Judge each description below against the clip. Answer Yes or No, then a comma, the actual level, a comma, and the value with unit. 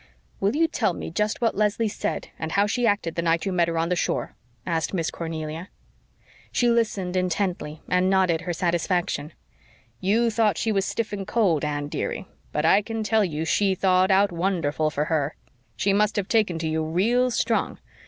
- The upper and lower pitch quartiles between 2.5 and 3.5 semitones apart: No, average, 4.2 semitones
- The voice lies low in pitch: No, medium, 185 Hz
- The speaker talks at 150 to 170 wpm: No, average, 195 wpm